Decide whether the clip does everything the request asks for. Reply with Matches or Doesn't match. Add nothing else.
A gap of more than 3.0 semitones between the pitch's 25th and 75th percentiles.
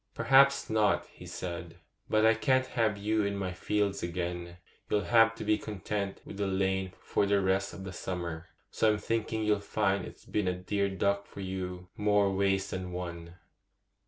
Doesn't match